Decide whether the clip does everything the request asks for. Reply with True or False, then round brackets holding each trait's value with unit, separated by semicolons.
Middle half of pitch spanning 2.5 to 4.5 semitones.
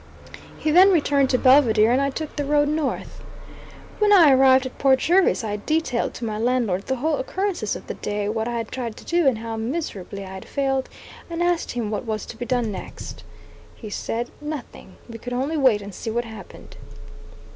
False (4.9 semitones)